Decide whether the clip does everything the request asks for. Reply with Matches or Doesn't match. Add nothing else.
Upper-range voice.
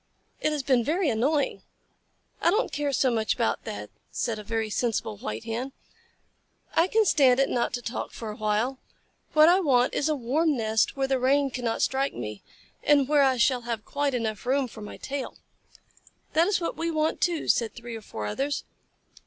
Matches